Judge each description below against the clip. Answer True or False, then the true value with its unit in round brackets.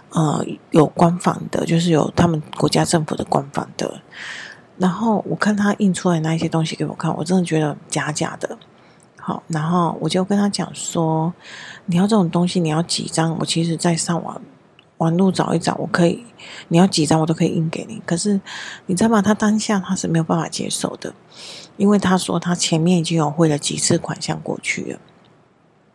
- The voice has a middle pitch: True (175 Hz)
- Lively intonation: False (2.6 semitones)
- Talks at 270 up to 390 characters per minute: True (285 characters per minute)